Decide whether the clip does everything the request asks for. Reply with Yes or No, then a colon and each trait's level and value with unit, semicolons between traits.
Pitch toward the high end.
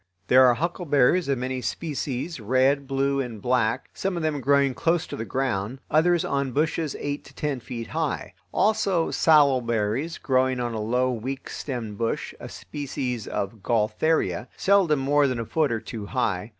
No: low, 130 Hz